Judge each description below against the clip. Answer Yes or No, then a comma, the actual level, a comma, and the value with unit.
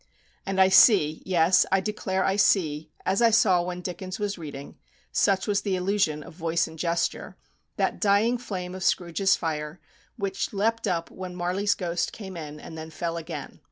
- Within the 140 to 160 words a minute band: No, average, 180 wpm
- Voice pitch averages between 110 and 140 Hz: No, medium, 185 Hz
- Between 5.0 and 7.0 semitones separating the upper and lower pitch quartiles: No, average, 3.0 semitones